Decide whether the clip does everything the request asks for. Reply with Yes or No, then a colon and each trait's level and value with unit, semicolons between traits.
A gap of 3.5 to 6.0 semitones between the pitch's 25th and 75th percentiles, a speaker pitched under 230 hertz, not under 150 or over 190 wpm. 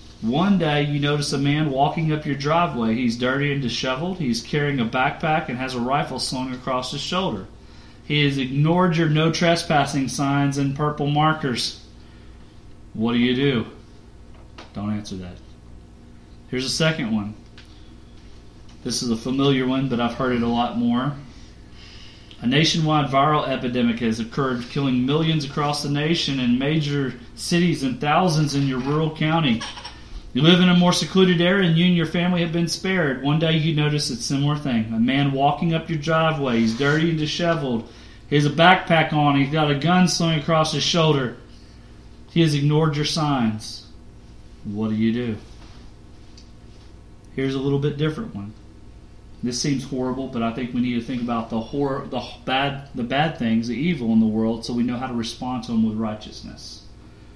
Yes: average, 4.7 semitones; low, 135 Hz; average, 180 wpm